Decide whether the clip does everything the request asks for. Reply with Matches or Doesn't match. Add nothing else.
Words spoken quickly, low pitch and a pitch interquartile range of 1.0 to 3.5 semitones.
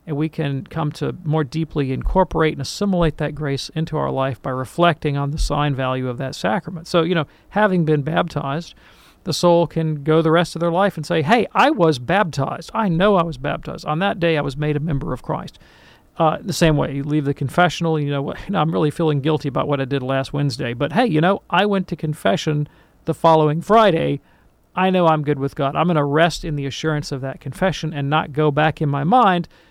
Doesn't match